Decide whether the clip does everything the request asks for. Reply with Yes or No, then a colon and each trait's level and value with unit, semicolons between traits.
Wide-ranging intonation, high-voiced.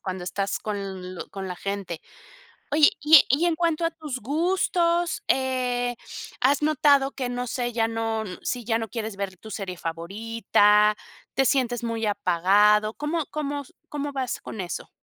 Yes: wide, 5.8 semitones; high, 230 Hz